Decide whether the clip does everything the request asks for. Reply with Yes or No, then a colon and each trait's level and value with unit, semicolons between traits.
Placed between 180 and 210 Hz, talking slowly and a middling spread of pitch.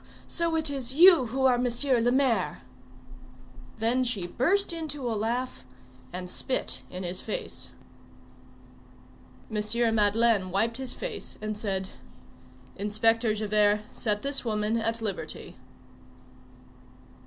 No: high, 230 Hz; slow, 120 wpm; average, 3.7 semitones